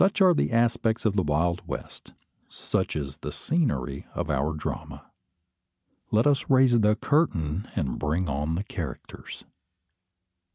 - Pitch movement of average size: No, wide, 8.1 semitones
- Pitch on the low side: Yes, very low, 90 Hz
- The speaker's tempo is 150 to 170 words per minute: No, average, 140 wpm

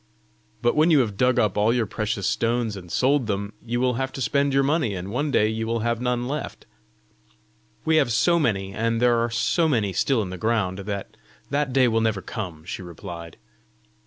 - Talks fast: Yes, fast, 210 wpm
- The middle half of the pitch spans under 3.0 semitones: No, average, 4.0 semitones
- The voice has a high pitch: No, low, 115 Hz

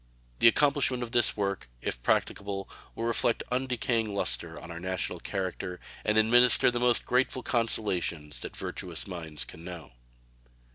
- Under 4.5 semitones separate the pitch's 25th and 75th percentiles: No, wide, 5.6 semitones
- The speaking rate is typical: Yes, average, 145 wpm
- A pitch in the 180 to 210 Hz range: No, low, 105 Hz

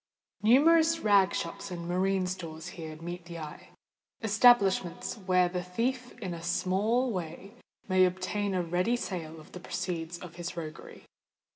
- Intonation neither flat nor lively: Yes, average, 3.3 semitones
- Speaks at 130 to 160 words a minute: Yes, average, 145 wpm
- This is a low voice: No, medium, 185 Hz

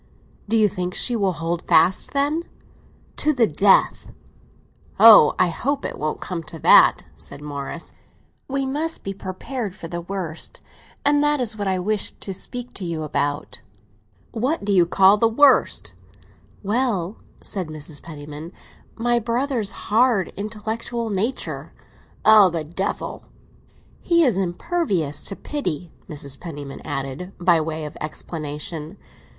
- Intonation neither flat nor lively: No, wide, 6.1 semitones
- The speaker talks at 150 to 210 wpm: No, average, 140 wpm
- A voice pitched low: No, high, 195 Hz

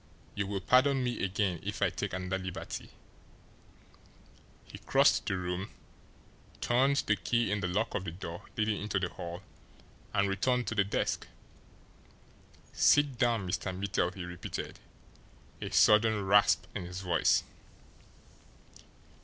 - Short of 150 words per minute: Yes, slow, 135 wpm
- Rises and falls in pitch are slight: No, average, 3.3 semitones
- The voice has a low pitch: Yes, low, 100 Hz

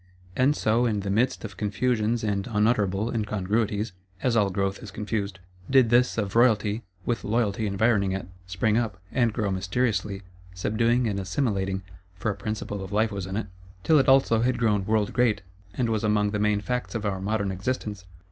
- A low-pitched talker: Yes, low, 105 Hz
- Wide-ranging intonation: No, average, 2.8 semitones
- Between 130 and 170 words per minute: No, average, 185 wpm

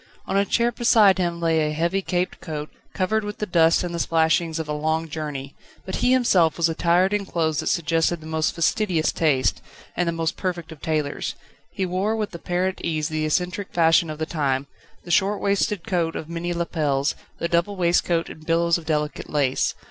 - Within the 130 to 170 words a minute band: No, average, 200 wpm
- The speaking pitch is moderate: Yes, medium, 170 Hz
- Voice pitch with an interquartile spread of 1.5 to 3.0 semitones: Yes, narrow, 2.6 semitones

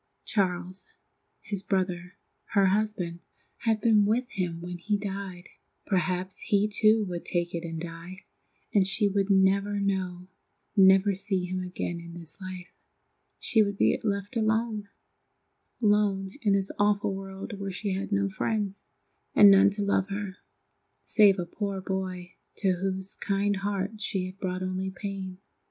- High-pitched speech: Yes, high, 195 Hz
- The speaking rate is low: No, average, 150 wpm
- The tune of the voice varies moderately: No, narrow, 1.8 semitones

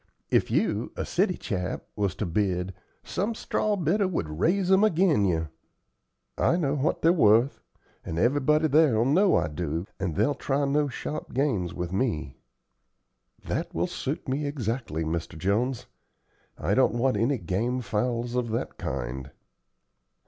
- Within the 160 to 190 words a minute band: No, average, 150 wpm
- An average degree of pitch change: No, wide, 8.3 semitones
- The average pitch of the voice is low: Yes, low, 120 Hz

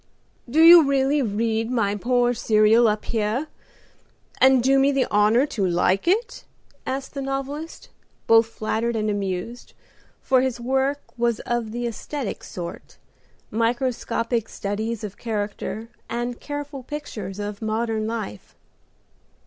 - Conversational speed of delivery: No, slow, 130 wpm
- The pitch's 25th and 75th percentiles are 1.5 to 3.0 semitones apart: No, average, 3.7 semitones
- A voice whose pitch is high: Yes, high, 235 Hz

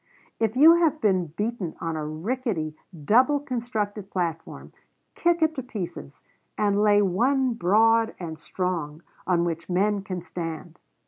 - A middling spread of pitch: No, wide, 5.8 semitones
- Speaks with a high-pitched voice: Yes, high, 205 Hz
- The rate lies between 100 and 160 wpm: Yes, average, 140 wpm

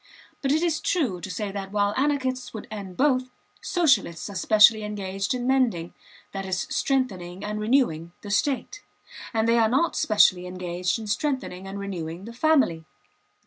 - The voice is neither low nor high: No, high, 210 Hz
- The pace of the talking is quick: No, average, 165 wpm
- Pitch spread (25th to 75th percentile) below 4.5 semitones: No, wide, 5.6 semitones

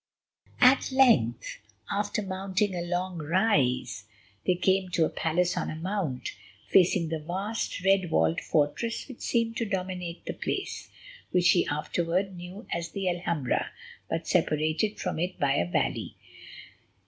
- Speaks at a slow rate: No, average, 145 wpm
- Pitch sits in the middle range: Yes, medium, 180 Hz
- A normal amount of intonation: Yes, average, 3.6 semitones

